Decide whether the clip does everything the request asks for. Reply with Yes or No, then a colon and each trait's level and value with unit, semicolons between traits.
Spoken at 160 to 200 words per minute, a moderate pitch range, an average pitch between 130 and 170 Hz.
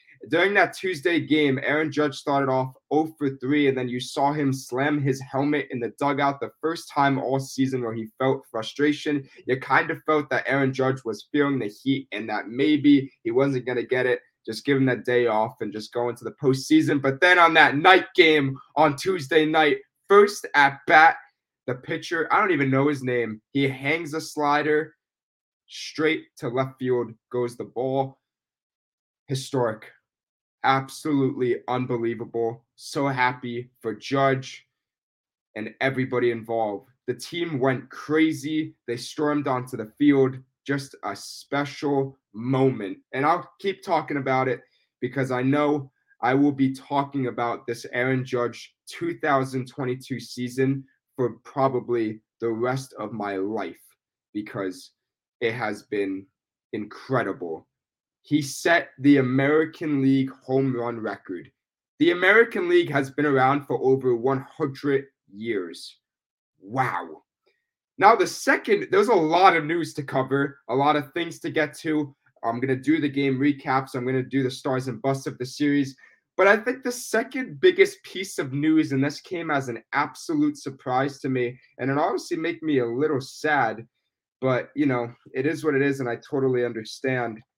Yes: average, 165 wpm; average, 3.1 semitones; low, 135 Hz